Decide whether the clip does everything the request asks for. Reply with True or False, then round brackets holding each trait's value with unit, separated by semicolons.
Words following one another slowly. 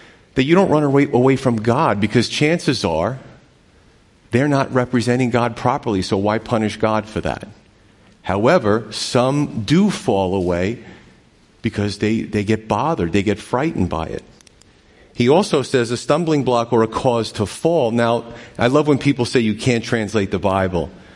False (165 wpm)